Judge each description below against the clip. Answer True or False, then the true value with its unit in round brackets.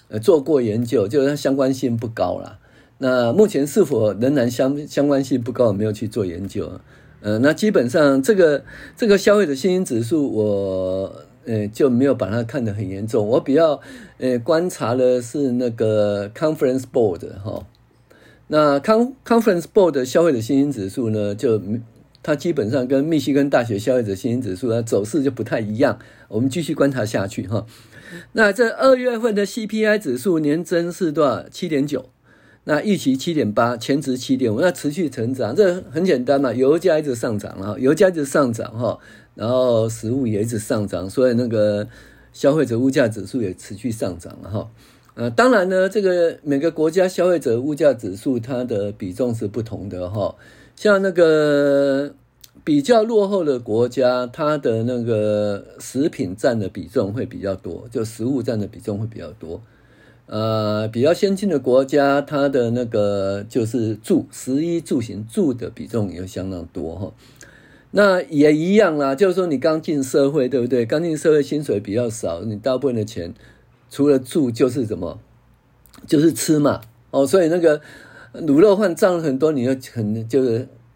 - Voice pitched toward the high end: False (130 Hz)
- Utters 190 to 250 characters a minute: False (280 characters per minute)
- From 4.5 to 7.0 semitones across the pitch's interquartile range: True (5.5 semitones)